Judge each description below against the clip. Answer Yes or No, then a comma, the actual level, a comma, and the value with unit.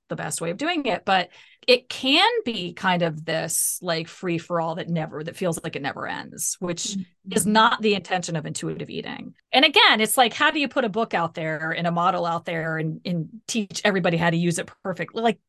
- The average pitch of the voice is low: No, medium, 180 Hz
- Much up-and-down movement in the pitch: No, average, 4.8 semitones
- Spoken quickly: Yes, fast, 230 wpm